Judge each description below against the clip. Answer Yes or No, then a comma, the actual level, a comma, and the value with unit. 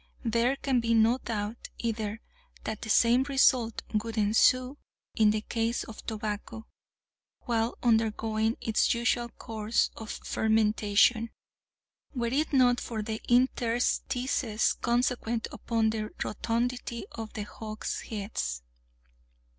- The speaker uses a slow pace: Yes, slow, 115 wpm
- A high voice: Yes, high, 225 Hz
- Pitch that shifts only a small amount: Yes, narrow, 1.7 semitones